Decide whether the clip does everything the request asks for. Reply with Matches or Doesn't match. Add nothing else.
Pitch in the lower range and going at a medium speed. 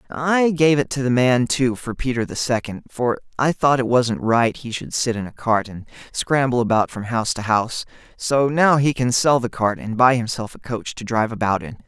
Doesn't match